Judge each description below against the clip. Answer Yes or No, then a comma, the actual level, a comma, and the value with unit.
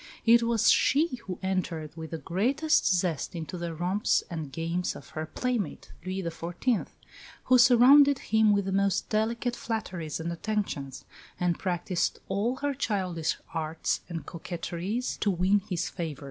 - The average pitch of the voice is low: No, medium, 185 Hz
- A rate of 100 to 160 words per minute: Yes, average, 150 wpm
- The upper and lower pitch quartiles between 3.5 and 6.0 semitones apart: Yes, average, 5.2 semitones